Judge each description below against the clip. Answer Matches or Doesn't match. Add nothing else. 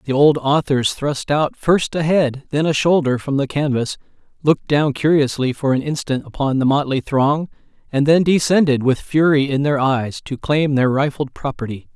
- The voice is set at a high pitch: Doesn't match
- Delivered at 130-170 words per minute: Doesn't match